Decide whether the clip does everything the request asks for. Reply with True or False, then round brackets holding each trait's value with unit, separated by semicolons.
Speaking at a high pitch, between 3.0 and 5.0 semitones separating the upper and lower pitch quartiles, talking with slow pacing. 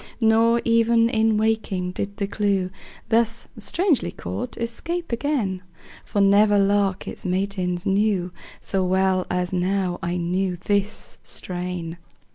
True (200 Hz; 3.4 semitones; 125 wpm)